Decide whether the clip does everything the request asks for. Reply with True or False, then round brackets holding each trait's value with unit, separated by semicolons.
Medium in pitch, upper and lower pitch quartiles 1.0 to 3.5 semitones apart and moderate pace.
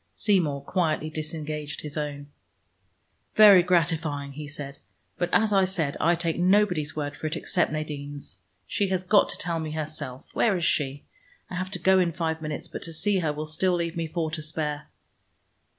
True (160 Hz; 3.1 semitones; 185 wpm)